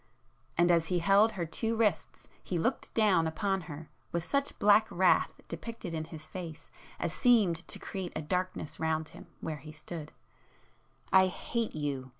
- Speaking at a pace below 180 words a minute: Yes, average, 160 wpm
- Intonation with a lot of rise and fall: No, average, 4.1 semitones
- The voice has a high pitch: No, medium, 175 Hz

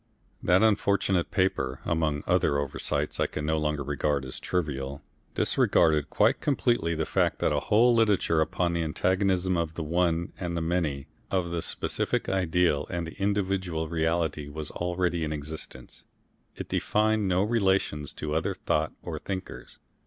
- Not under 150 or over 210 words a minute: Yes, average, 155 wpm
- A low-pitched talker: Yes, very low, 85 Hz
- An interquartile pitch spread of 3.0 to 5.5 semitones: Yes, average, 3.5 semitones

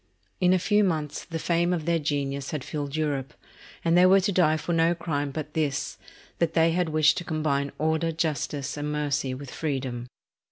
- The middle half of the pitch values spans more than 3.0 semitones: No, average, 2.7 semitones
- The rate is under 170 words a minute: No, average, 195 wpm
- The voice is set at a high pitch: No, medium, 155 Hz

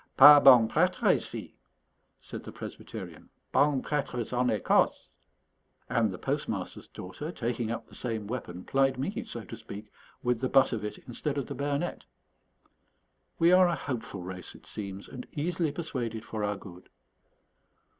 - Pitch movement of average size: Yes, average, 4.8 semitones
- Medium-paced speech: Yes, average, 155 wpm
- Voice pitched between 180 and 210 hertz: No, low, 125 Hz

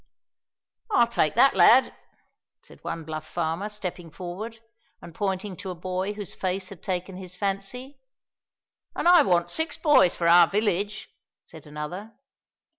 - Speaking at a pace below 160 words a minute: Yes, average, 145 wpm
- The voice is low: No, high, 190 Hz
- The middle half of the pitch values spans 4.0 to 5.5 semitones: No, average, 3.4 semitones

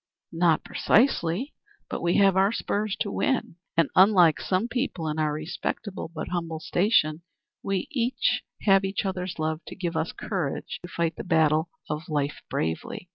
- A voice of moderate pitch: Yes, medium, 175 Hz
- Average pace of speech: Yes, average, 160 wpm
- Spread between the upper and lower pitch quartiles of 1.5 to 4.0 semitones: Yes, average, 3.6 semitones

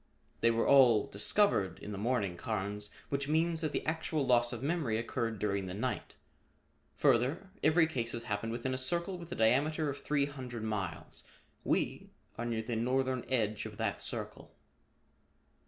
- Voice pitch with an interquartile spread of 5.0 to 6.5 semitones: No, average, 4.6 semitones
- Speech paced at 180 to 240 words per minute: No, average, 170 wpm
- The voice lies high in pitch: No, low, 120 Hz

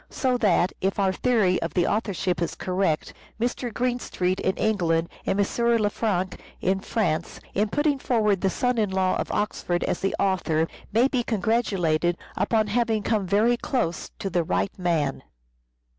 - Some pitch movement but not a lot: Yes, average, 4.1 semitones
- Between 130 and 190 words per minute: Yes, average, 160 wpm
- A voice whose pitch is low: No, high, 195 Hz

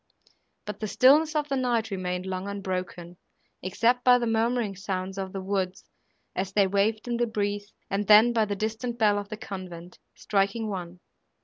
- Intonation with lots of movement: No, average, 3.2 semitones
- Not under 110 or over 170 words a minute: No, average, 180 wpm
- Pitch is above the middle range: Yes, high, 205 Hz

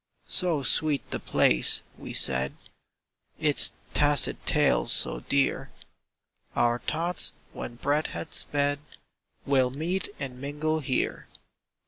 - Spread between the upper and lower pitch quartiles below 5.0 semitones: Yes, average, 3.6 semitones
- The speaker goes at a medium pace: No, slow, 110 wpm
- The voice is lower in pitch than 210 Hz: Yes, medium, 140 Hz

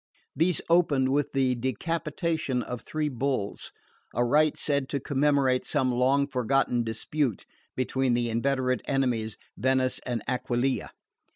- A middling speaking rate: No, slow, 125 wpm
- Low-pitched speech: Yes, low, 130 Hz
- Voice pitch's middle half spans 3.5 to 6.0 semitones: No, narrow, 2.5 semitones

